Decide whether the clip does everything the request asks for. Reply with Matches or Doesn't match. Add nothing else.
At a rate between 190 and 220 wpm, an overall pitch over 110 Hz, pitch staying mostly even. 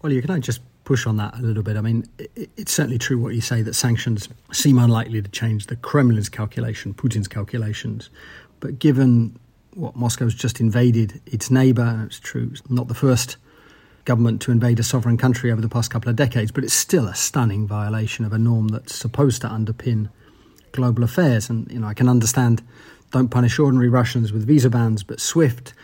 Matches